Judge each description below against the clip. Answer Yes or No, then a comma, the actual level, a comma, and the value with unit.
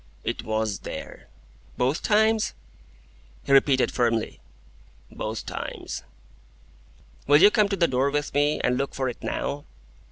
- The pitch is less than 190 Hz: Yes, medium, 140 Hz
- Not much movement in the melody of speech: No, average, 4.4 semitones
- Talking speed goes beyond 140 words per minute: No, slow, 135 wpm